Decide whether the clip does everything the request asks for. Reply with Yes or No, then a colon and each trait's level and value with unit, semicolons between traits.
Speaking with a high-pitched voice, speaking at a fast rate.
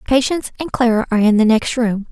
Yes: high, 235 Hz; fast, 225 wpm